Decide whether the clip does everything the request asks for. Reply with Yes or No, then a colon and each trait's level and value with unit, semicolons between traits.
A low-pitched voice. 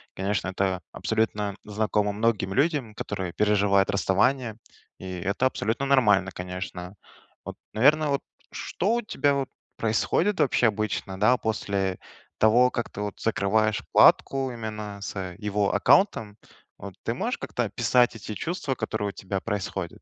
Yes: low, 105 Hz